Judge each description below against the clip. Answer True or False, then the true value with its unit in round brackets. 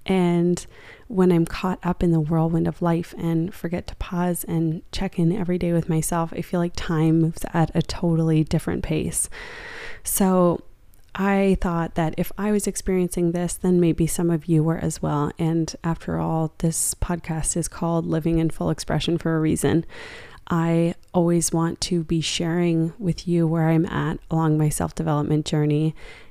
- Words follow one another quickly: False (180 wpm)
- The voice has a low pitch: False (170 Hz)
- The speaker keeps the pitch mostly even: True (1.5 semitones)